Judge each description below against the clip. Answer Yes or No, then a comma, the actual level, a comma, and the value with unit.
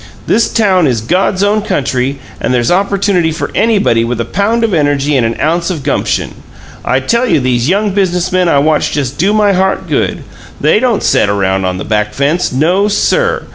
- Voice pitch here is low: No, medium, 170 Hz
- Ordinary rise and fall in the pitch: No, wide, 7.7 semitones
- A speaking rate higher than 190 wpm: Yes, average, 200 wpm